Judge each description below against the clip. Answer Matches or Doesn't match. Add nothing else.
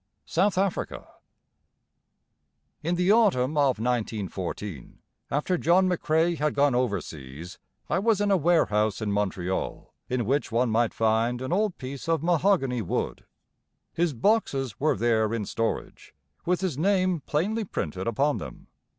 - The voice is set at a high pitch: Doesn't match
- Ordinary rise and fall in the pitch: Doesn't match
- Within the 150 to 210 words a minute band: Doesn't match